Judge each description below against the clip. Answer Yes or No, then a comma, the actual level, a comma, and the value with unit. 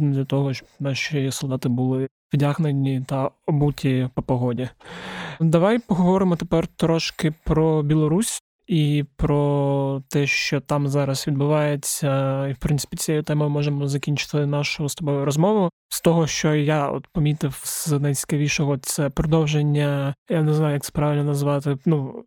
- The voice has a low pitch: No, medium, 145 Hz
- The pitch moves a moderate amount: No, narrow, 2.0 semitones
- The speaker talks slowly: No, average, 145 wpm